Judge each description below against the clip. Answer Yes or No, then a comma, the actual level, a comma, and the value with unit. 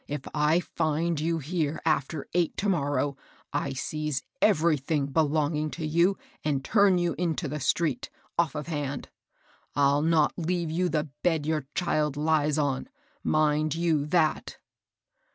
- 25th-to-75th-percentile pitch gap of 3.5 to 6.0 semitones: No, narrow, 2.4 semitones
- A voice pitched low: No, medium, 155 Hz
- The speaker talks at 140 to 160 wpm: Yes, average, 155 wpm